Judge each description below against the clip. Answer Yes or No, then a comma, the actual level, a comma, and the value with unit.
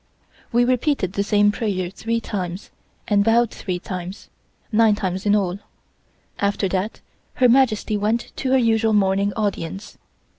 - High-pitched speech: Yes, high, 205 Hz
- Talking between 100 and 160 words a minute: Yes, average, 145 wpm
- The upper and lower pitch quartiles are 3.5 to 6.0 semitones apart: No, average, 2.9 semitones